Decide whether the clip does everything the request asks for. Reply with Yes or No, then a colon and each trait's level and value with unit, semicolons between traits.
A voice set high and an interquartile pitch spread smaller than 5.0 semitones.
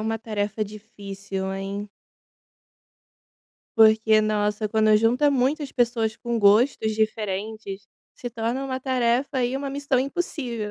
Yes: high, 220 Hz; average, 3.1 semitones